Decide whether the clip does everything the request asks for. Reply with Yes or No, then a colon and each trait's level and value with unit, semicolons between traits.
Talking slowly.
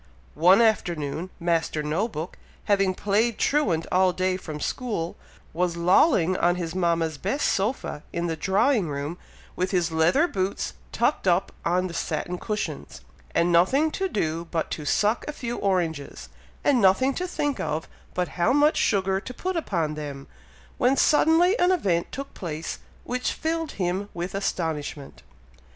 No: average, 155 wpm